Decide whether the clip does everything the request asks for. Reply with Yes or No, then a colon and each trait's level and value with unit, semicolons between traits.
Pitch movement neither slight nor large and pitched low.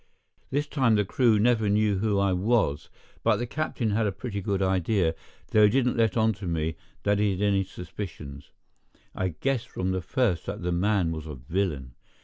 Yes: average, 3.9 semitones; low, 100 Hz